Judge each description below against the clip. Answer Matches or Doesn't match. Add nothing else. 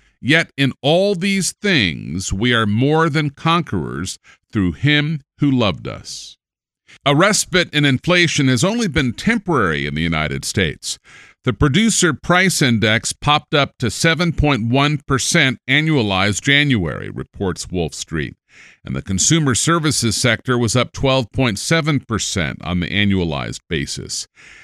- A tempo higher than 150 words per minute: Doesn't match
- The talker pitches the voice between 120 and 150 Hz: Matches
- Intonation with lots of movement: Matches